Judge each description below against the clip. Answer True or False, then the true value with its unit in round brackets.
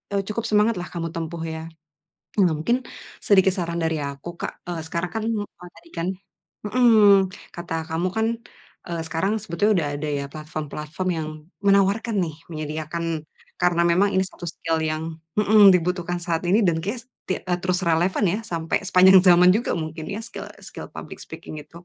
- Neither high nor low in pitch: True (175 Hz)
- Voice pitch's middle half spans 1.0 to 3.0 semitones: False (3.5 semitones)